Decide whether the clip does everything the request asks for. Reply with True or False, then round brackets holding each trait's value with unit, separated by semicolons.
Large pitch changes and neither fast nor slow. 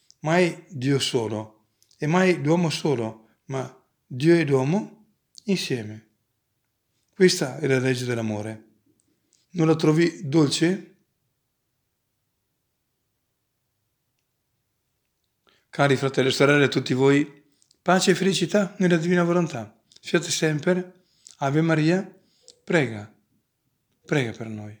False (5.8 semitones; 100 wpm)